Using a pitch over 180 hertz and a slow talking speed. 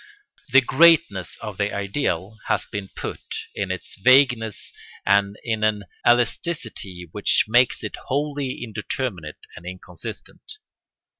No: low, 105 Hz; slow, 120 wpm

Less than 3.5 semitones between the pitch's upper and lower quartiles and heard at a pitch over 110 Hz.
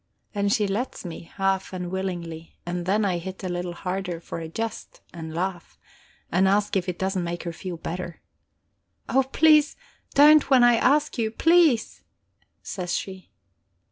No: average, 4.0 semitones; high, 190 Hz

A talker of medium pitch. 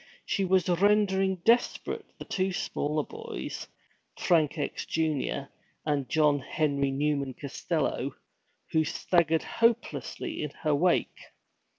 Yes: medium, 160 Hz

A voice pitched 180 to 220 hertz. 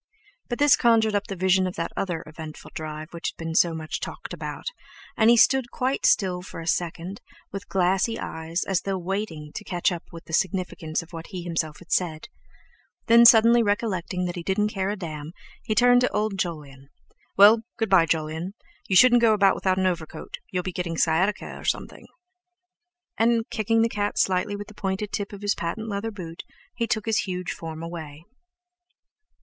Yes: high, 190 Hz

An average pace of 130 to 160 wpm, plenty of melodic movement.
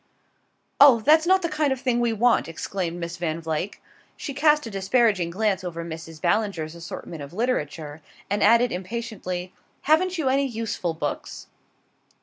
Yes: average, 155 wpm; wide, 6.9 semitones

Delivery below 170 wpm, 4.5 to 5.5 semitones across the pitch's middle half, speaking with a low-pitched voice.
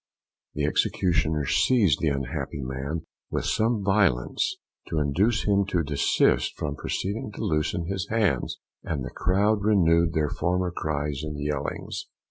Yes: average, 140 wpm; average, 5.2 semitones; very low, 85 Hz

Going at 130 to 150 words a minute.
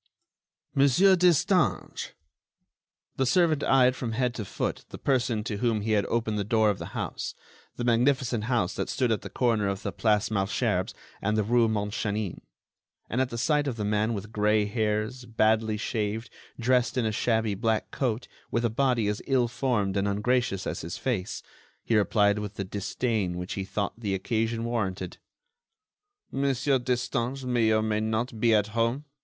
No: average, 170 wpm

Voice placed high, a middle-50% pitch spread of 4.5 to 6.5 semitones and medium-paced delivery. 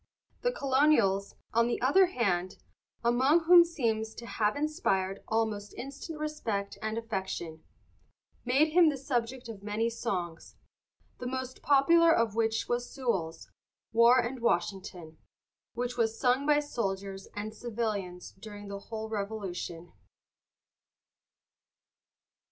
No: high, 230 Hz; average, 4.8 semitones; slow, 125 wpm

